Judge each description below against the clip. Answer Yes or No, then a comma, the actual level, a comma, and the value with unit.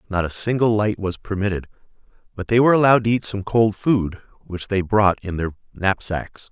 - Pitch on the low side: Yes, low, 100 Hz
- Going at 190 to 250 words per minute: Yes, average, 195 wpm